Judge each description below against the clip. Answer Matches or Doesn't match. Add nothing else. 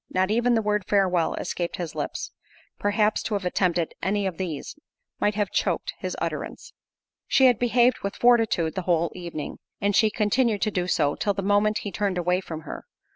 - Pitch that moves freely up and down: Doesn't match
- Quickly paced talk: Doesn't match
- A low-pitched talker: Doesn't match